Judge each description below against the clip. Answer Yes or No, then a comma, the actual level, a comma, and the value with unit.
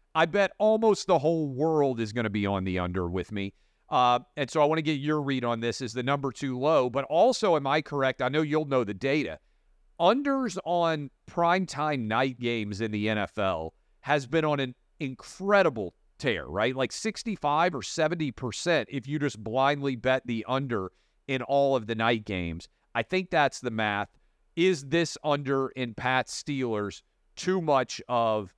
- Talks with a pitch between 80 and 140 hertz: Yes, low, 135 Hz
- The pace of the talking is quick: No, average, 185 wpm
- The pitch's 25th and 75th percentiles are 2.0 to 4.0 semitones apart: No, average, 5.0 semitones